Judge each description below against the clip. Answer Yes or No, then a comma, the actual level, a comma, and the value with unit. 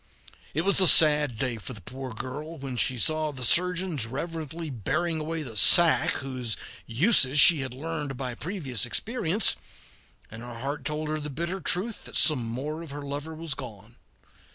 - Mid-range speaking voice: Yes, medium, 145 Hz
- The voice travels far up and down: No, average, 4.3 semitones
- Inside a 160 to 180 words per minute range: Yes, average, 175 wpm